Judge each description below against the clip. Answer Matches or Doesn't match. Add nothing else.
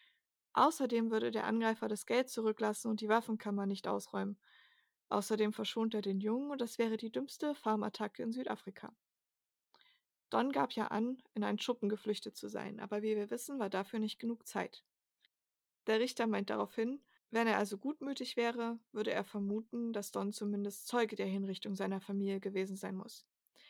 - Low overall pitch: Doesn't match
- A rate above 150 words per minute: Matches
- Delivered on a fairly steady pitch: Matches